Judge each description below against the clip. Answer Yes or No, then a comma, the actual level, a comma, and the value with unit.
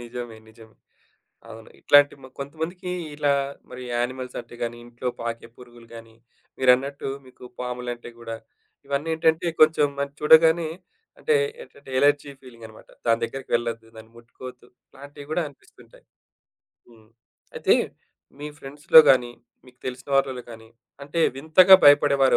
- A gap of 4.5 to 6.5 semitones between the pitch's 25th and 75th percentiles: No, average, 3.4 semitones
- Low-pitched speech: Yes, low, 130 Hz